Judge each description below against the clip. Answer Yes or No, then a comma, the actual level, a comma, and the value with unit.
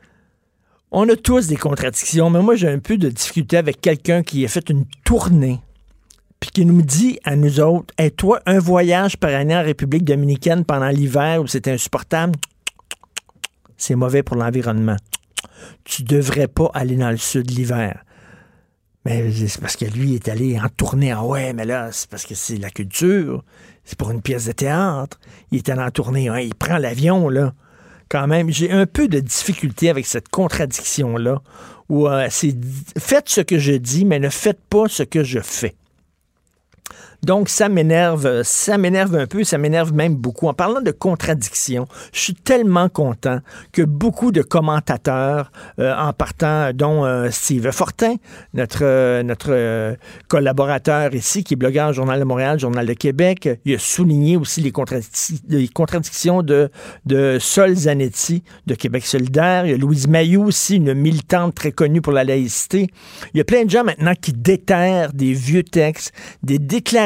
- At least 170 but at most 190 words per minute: Yes, average, 185 wpm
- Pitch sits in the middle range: Yes, medium, 145 Hz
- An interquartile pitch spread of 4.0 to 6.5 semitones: Yes, average, 5.2 semitones